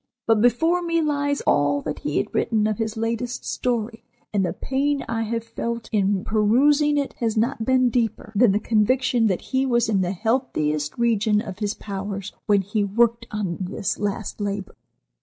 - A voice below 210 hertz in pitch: No, high, 225 Hz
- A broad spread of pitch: No, average, 3.3 semitones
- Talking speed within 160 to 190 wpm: Yes, average, 180 wpm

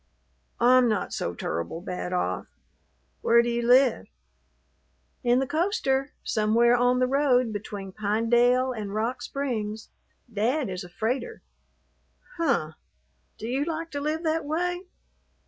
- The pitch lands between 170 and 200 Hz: No, high, 245 Hz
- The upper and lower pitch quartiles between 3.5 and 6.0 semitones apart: Yes, average, 4.3 semitones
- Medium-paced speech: No, slow, 130 wpm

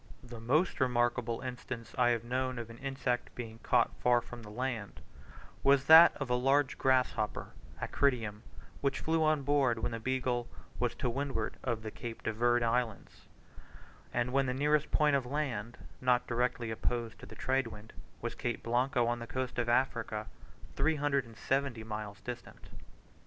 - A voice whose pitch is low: Yes, low, 125 Hz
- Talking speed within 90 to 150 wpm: No, average, 165 wpm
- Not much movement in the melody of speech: Yes, narrow, 2.3 semitones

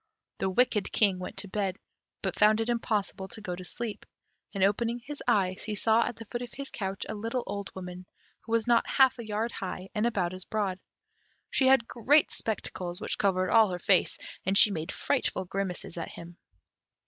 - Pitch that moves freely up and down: No, average, 3.5 semitones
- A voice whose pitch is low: No, high, 205 Hz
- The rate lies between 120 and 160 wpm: No, average, 200 wpm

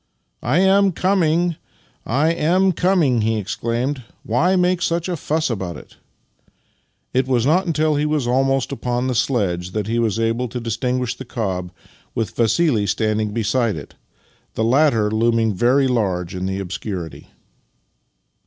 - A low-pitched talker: Yes, low, 120 Hz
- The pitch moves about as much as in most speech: No, wide, 6.0 semitones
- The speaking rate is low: No, average, 165 wpm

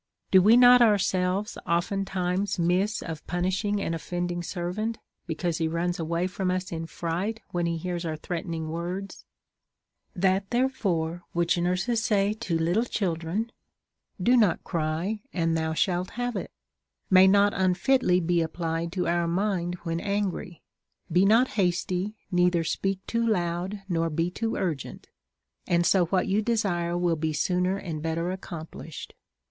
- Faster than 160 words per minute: No, average, 155 wpm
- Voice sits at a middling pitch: Yes, medium, 180 Hz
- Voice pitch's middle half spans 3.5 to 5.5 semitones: No, average, 2.8 semitones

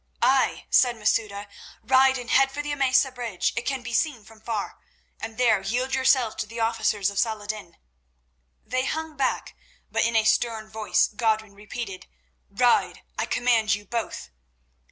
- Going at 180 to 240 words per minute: No, average, 160 wpm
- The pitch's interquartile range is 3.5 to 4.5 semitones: No, average, 3.1 semitones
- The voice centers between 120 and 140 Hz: No, high, 230 Hz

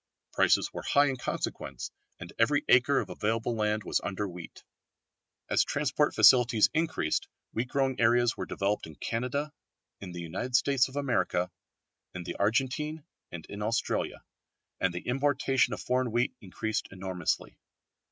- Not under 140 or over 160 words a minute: Yes, average, 150 wpm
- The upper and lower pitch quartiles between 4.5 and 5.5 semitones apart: Yes, average, 4.9 semitones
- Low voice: Yes, low, 120 Hz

